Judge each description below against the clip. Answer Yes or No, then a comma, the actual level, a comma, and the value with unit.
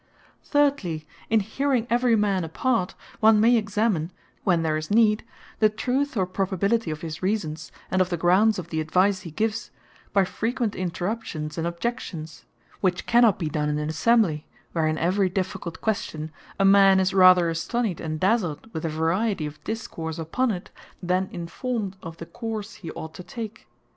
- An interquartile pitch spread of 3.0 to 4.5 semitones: No, average, 5.2 semitones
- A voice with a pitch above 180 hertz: Yes, high, 190 Hz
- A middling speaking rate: Yes, average, 175 wpm